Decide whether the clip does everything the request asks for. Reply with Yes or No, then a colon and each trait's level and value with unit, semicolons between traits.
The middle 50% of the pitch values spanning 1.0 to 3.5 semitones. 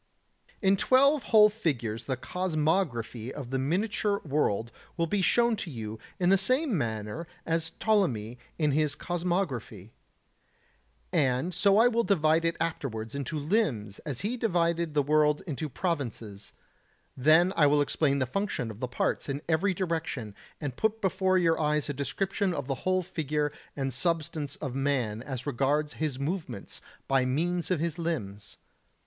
No: wide, 5.6 semitones